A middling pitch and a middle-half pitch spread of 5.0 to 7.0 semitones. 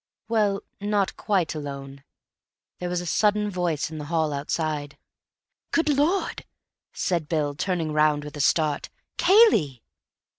Yes: medium, 165 Hz; wide, 5.5 semitones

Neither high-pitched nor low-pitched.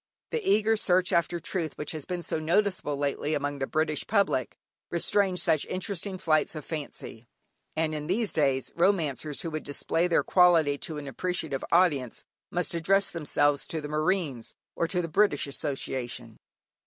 Yes: medium, 160 Hz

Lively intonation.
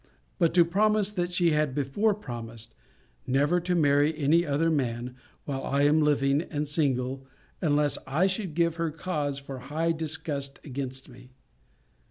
No: average, 3.6 semitones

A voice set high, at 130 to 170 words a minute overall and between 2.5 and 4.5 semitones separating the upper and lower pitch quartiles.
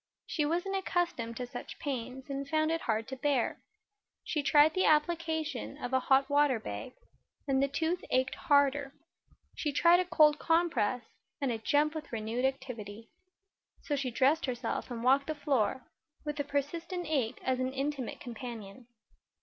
Yes: very high, 275 Hz; average, 165 wpm; average, 3.7 semitones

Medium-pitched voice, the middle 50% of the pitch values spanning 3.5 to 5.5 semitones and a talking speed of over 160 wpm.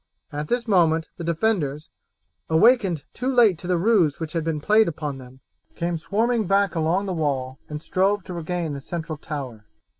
Yes: medium, 170 Hz; average, 4.7 semitones; average, 180 wpm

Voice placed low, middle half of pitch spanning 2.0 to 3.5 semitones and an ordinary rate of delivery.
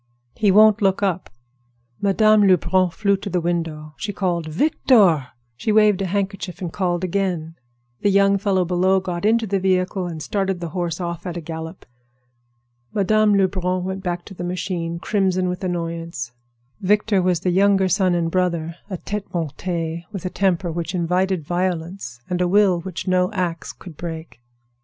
No: medium, 185 Hz; narrow, 2.4 semitones; average, 165 wpm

